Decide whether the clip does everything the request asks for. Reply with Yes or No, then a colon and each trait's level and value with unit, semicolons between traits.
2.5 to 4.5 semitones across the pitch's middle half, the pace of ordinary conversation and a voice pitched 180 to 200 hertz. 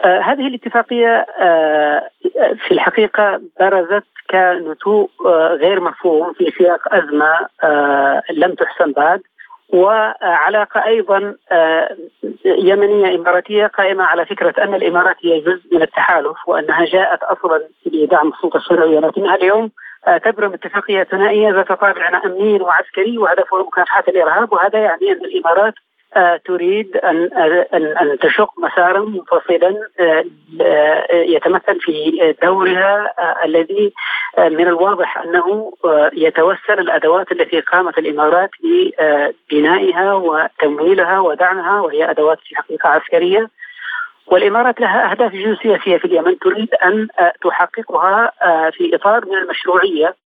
Yes: average, 4.0 semitones; average, 110 wpm; high, 190 Hz